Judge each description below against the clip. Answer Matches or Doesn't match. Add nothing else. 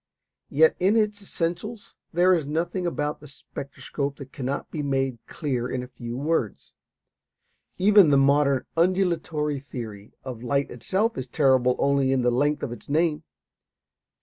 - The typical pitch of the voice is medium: Matches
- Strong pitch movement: Doesn't match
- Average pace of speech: Matches